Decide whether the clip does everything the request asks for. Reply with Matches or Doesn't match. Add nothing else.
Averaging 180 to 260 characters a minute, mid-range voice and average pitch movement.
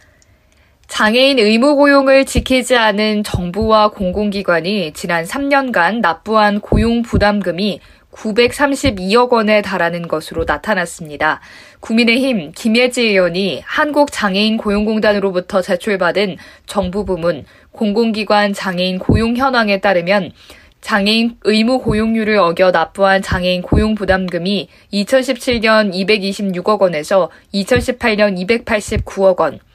Doesn't match